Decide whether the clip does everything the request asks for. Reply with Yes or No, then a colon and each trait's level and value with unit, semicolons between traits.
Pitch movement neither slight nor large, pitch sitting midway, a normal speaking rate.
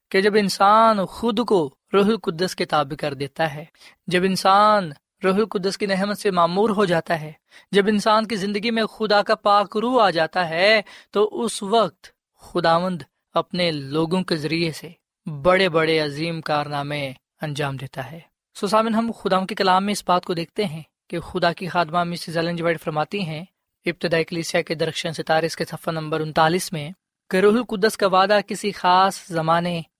Yes: average, 3.9 semitones; medium, 180 Hz; average, 175 wpm